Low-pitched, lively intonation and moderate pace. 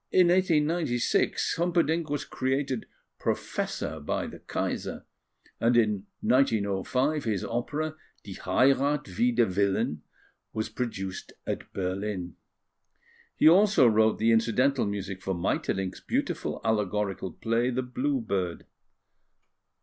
No: low, 115 Hz; wide, 6.1 semitones; slow, 110 wpm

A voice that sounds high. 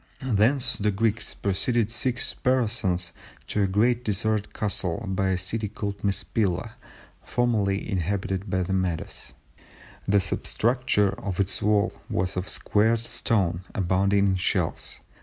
No: low, 100 Hz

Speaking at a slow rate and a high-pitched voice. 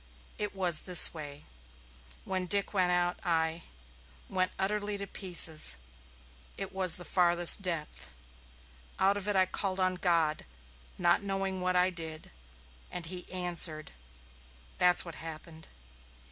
No: slow, 130 wpm; medium, 180 Hz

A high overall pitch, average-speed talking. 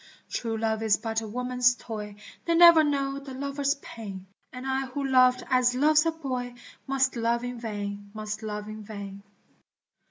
Yes: high, 245 Hz; average, 170 wpm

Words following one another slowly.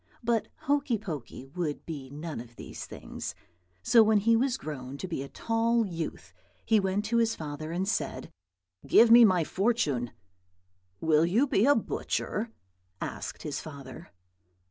No: average, 155 wpm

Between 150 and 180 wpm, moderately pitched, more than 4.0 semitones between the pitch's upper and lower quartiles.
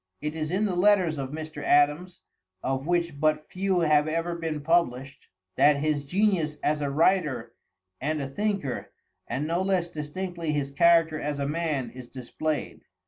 No: average, 165 wpm; medium, 155 Hz; average, 3.0 semitones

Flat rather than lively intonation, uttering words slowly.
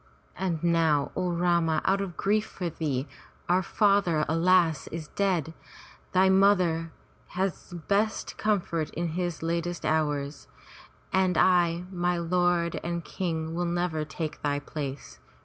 Yes: narrow, 2.3 semitones; slow, 130 wpm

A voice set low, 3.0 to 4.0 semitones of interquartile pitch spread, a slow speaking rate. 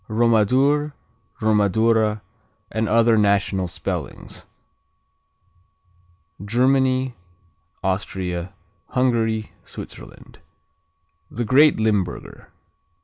Yes: low, 110 Hz; average, 3.7 semitones; slow, 60 wpm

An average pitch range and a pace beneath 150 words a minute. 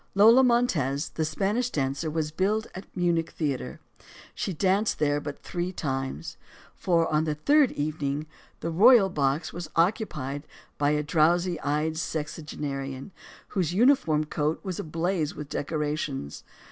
Yes: average, 4.1 semitones; average, 140 wpm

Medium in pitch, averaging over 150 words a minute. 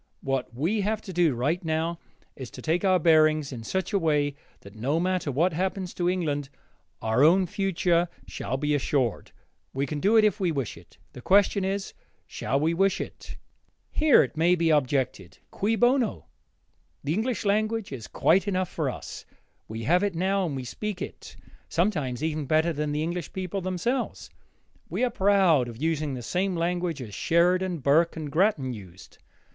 Yes: medium, 165 Hz; average, 180 wpm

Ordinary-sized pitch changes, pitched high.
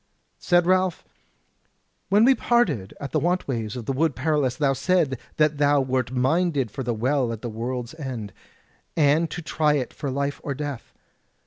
No: average, 4.2 semitones; medium, 140 Hz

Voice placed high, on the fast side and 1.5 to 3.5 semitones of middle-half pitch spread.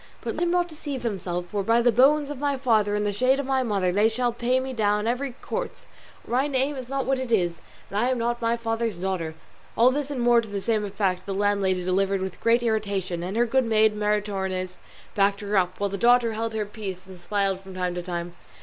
No: high, 215 Hz; fast, 240 wpm; average, 4.3 semitones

